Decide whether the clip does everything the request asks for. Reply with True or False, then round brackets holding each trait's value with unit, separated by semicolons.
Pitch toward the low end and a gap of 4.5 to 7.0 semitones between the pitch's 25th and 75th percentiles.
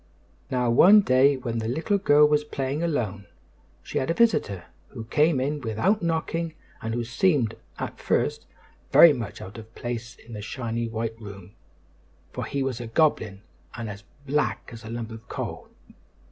True (120 Hz; 4.8 semitones)